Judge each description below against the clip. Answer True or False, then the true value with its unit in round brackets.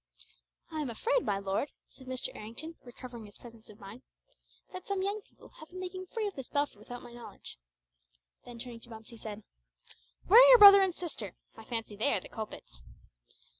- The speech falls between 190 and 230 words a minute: True (200 wpm)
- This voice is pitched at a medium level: False (245 Hz)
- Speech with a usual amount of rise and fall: False (9.0 semitones)